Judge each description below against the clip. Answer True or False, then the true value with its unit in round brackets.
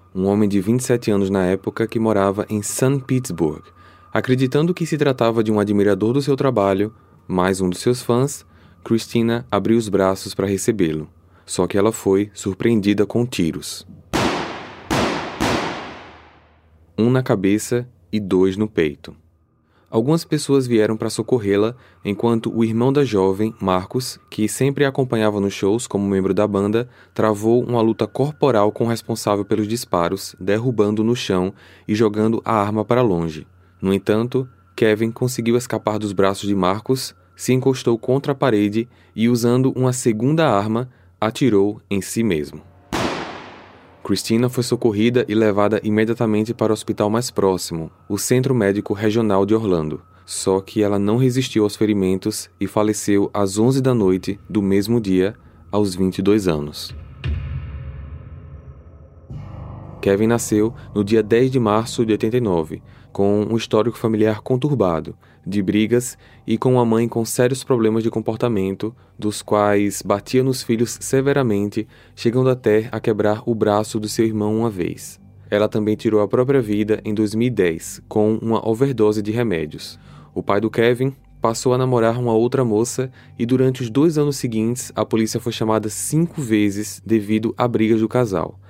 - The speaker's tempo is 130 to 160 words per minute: True (155 wpm)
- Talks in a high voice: False (110 Hz)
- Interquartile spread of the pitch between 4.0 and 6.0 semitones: False (3.3 semitones)